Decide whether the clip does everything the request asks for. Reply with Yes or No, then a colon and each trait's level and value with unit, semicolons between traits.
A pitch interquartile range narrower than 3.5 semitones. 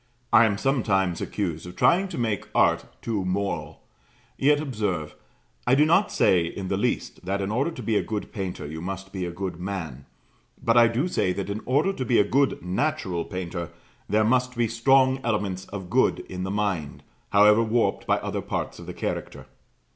No: average, 4.7 semitones